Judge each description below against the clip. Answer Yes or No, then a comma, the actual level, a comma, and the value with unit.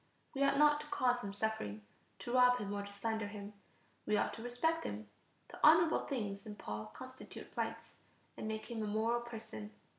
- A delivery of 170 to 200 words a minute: Yes, average, 190 wpm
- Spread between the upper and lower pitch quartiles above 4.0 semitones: No, average, 3.7 semitones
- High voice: Yes, high, 220 Hz